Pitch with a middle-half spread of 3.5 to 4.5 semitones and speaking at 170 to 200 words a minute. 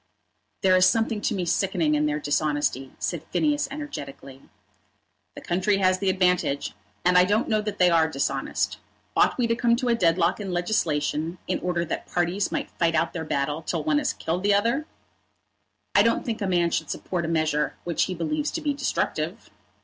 No: average, 5.1 semitones; average, 195 wpm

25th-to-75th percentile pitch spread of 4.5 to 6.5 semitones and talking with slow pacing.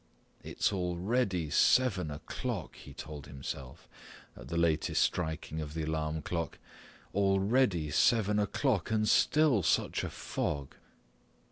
Yes: average, 5.3 semitones; slow, 120 wpm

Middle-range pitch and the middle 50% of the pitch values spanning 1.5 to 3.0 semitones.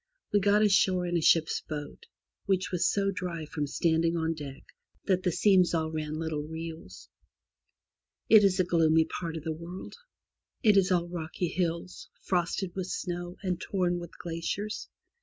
Yes: medium, 175 Hz; narrow, 2.4 semitones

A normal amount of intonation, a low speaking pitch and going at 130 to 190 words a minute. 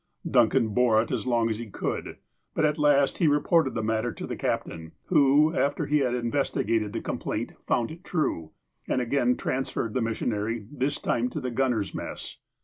No: average, 4.1 semitones; low, 125 Hz; average, 200 wpm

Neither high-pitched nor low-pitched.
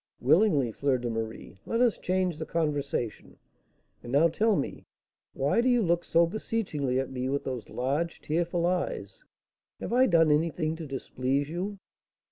Yes: medium, 155 Hz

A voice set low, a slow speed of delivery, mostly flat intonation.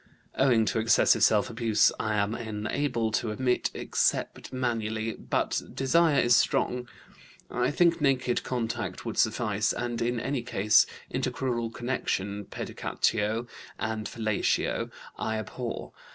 Yes: low, 115 Hz; slow, 125 wpm; narrow, 2.3 semitones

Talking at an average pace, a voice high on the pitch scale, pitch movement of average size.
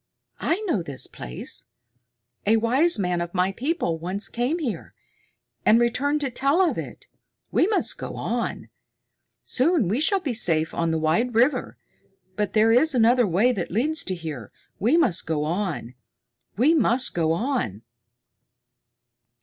No: average, 150 wpm; high, 225 Hz; wide, 8.2 semitones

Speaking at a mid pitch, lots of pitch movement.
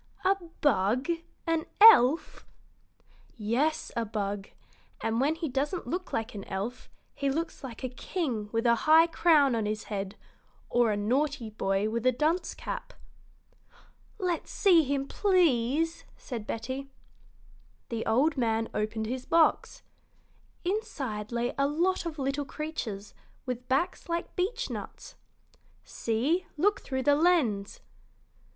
No: very high, 265 Hz; wide, 6.4 semitones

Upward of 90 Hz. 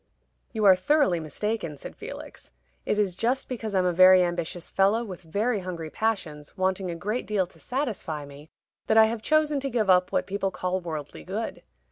Yes: high, 190 Hz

